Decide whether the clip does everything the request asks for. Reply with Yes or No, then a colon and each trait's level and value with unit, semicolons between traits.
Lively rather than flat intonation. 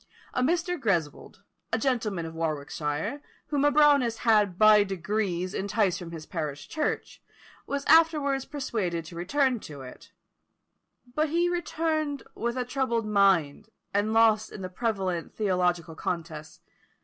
Yes: wide, 8.0 semitones